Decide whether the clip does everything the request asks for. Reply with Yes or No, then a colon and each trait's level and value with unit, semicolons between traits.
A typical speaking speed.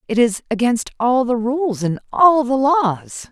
Yes: average, 180 wpm